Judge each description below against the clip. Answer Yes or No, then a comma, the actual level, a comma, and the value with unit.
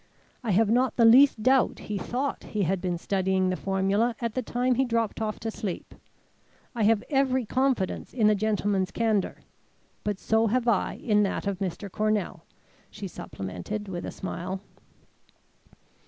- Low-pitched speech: No, high, 215 Hz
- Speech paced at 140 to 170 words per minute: Yes, average, 165 wpm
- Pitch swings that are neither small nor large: Yes, average, 3.5 semitones